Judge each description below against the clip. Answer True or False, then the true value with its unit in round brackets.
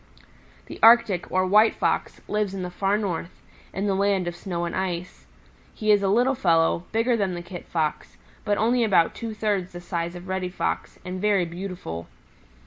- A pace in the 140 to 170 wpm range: False (190 wpm)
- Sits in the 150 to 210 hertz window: True (190 Hz)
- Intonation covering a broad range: False (3.1 semitones)